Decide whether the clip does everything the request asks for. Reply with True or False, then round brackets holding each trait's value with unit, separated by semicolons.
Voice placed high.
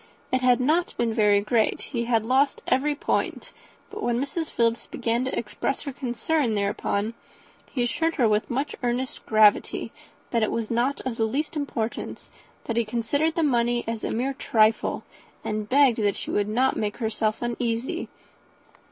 True (240 Hz)